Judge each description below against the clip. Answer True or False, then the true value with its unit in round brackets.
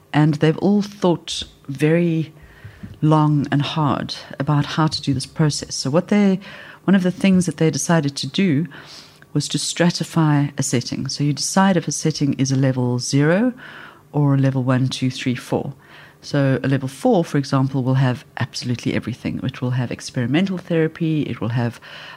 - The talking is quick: False (180 wpm)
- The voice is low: False (145 Hz)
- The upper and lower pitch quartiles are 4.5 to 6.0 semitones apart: False (3.7 semitones)